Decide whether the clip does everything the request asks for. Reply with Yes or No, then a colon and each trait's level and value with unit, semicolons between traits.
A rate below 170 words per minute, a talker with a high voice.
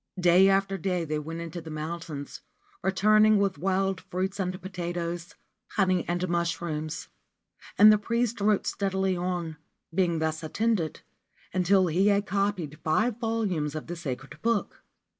No: average, 140 wpm; medium, 180 Hz